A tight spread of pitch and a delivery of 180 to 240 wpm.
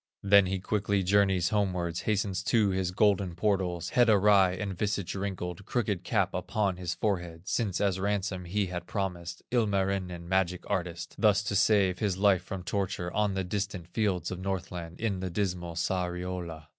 No: narrow, 2.3 semitones; average, 165 wpm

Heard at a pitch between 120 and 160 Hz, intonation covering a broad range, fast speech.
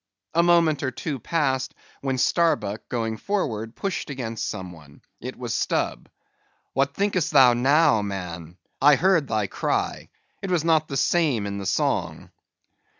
No: low, 135 Hz; wide, 7.0 semitones; average, 150 wpm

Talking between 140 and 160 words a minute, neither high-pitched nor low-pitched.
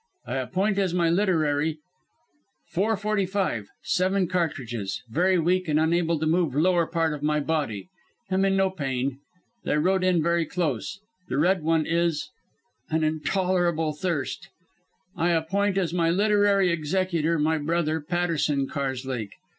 Yes: average, 145 wpm; medium, 165 Hz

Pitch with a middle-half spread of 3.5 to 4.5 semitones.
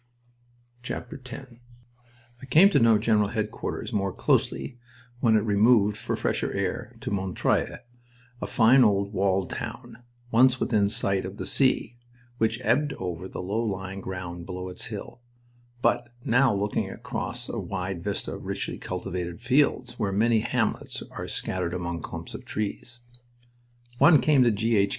Yes: average, 3.8 semitones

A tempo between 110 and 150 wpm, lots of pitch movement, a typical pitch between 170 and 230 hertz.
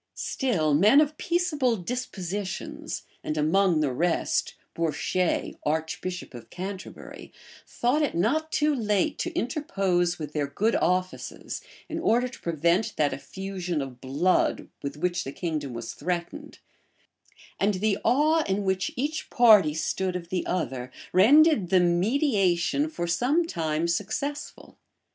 Yes: slow, 135 wpm; wide, 6.7 semitones; medium, 185 Hz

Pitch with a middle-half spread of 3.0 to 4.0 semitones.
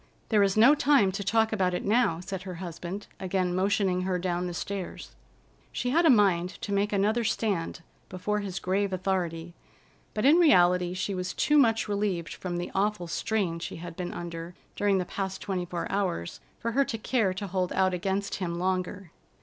No: narrow, 2.6 semitones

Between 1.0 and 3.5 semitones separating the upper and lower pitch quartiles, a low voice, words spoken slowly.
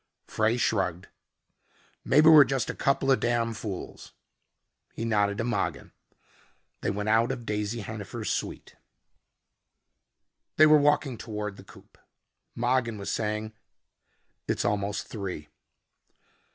Yes: average, 2.9 semitones; low, 110 Hz; slow, 120 wpm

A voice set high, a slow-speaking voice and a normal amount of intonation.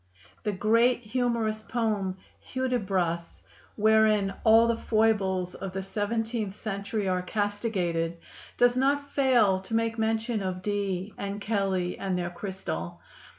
Yes: high, 210 Hz; slow, 125 wpm; average, 3.1 semitones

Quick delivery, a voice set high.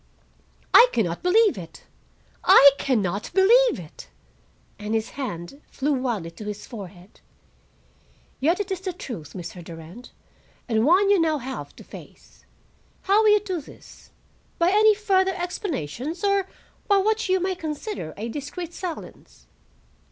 No: average, 150 wpm; very high, 305 Hz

